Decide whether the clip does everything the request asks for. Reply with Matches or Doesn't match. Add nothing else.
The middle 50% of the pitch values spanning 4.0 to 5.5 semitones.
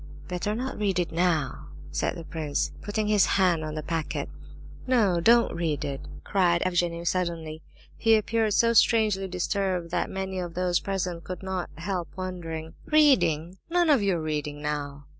Doesn't match